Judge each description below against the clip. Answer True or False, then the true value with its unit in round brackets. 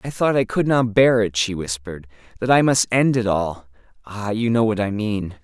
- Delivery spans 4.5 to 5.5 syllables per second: True (5.0 syllables/s)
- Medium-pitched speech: False (110 Hz)